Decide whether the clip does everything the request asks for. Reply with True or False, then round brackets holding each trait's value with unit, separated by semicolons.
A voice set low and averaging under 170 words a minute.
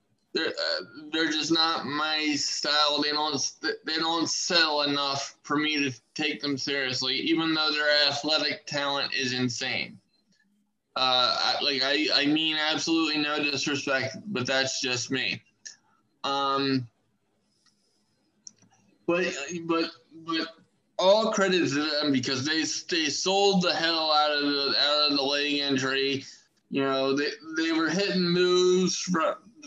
False (150 Hz; 140 wpm)